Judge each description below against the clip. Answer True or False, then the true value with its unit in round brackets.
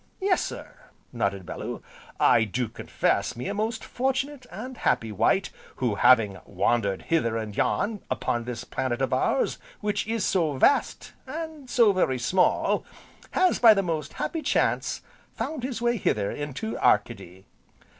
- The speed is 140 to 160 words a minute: True (150 wpm)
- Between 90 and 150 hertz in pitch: False (165 Hz)